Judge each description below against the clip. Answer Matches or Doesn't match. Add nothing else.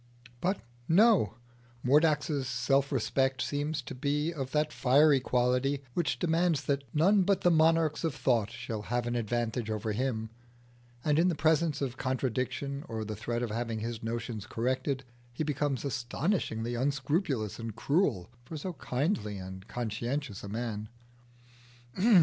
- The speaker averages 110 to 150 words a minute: Matches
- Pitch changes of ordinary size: Matches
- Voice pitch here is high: Doesn't match